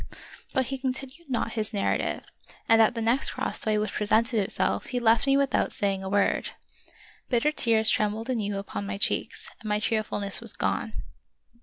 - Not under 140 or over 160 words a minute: No, average, 175 wpm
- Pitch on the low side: No, high, 225 Hz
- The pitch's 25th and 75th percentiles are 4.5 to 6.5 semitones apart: No, average, 3.3 semitones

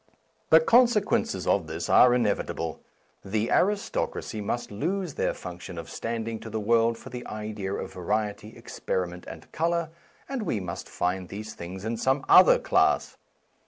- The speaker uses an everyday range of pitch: No, wide, 6.2 semitones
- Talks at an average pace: Yes, average, 155 wpm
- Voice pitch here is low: Yes, low, 110 Hz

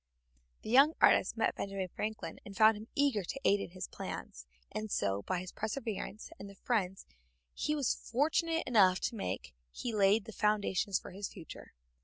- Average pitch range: Yes, average, 3.4 semitones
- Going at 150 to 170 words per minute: No, average, 185 wpm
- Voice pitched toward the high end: Yes, high, 210 Hz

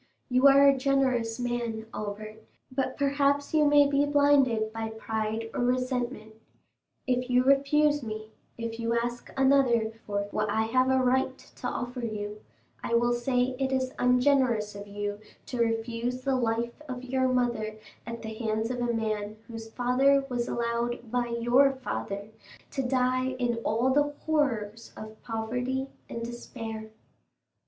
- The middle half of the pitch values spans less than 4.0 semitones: Yes, average, 2.8 semitones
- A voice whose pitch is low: No, high, 240 Hz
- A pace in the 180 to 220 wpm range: No, average, 155 wpm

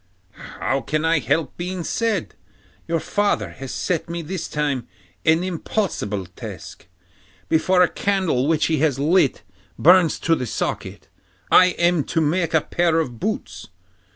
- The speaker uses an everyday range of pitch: Yes, average, 3.8 semitones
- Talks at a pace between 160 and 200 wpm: No, average, 150 wpm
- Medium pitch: Yes, medium, 165 Hz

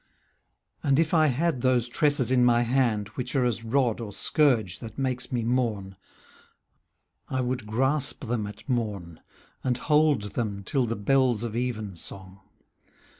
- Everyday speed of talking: Yes, average, 150 wpm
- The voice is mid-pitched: No, low, 120 Hz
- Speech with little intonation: No, average, 3.4 semitones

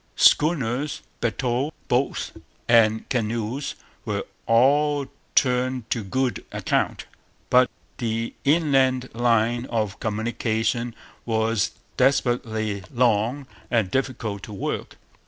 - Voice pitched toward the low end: Yes, low, 120 Hz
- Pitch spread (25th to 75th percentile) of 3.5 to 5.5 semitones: No, average, 2.8 semitones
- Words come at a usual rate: No, slow, 95 wpm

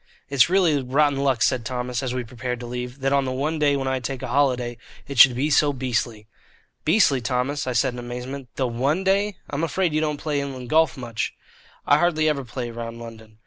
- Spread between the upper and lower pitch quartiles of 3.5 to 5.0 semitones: No, average, 2.9 semitones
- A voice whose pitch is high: No, low, 130 Hz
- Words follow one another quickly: Yes, fast, 220 wpm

